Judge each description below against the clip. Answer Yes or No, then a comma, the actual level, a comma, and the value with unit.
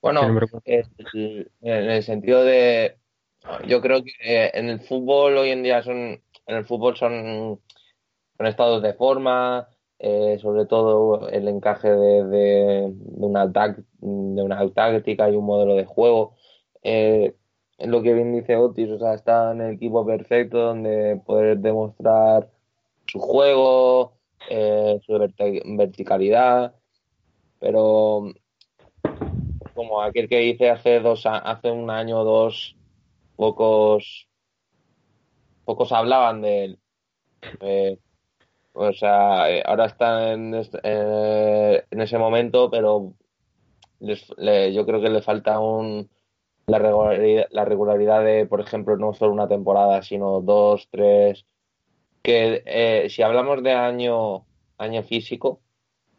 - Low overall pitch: Yes, low, 110 Hz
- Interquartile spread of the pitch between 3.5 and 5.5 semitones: No, narrow, 2.4 semitones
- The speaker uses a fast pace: No, average, 130 wpm